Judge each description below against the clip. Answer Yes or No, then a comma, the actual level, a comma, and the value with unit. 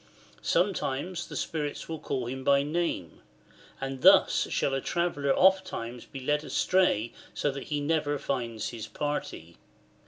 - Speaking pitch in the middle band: Yes, medium, 145 Hz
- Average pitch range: Yes, average, 3.8 semitones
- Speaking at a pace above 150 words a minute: No, average, 145 wpm